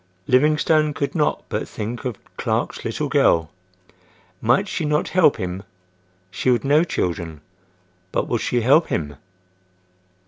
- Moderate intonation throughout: No, wide, 8.3 semitones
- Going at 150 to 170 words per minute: No, slow, 135 wpm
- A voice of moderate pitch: No, low, 125 Hz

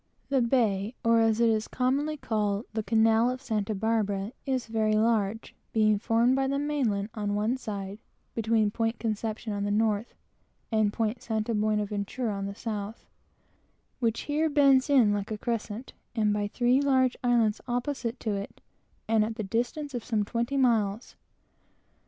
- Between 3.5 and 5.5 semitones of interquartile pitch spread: No, average, 2.7 semitones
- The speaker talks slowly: No, average, 165 wpm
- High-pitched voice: Yes, high, 225 Hz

